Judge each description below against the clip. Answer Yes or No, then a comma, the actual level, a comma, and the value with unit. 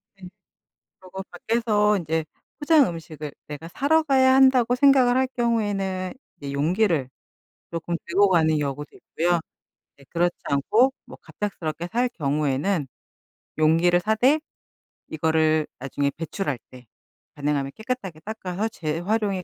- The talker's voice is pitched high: No, medium, 180 Hz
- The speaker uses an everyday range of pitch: No, wide, 6.2 semitones